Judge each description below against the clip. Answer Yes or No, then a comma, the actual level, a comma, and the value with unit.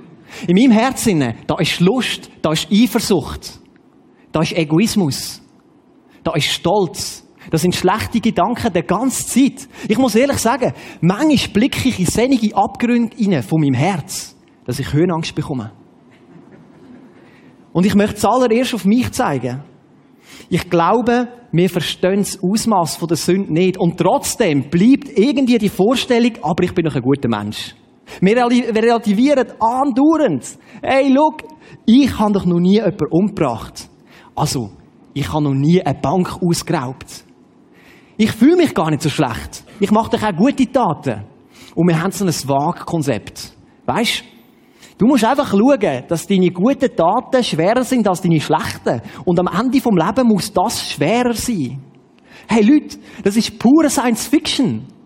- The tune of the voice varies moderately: No, wide, 6.8 semitones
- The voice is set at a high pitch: Yes, high, 195 Hz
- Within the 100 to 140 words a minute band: No, average, 150 wpm